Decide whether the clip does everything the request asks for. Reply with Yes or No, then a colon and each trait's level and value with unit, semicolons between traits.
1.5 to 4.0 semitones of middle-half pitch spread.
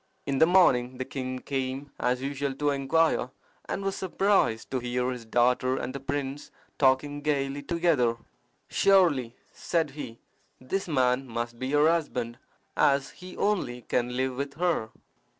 Yes: average, 3.1 semitones